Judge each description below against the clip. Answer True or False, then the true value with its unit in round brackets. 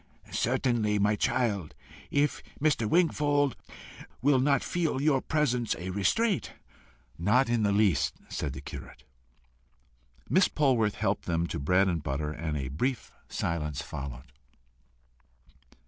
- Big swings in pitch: True (8.6 semitones)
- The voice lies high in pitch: False (110 Hz)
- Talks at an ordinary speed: False (125 wpm)